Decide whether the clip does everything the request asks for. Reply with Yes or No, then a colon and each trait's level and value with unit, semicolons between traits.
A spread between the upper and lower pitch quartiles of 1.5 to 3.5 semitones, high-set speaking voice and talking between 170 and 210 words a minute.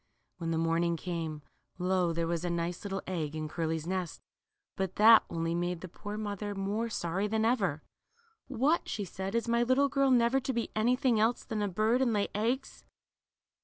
No: average, 5.3 semitones; high, 195 Hz; average, 190 wpm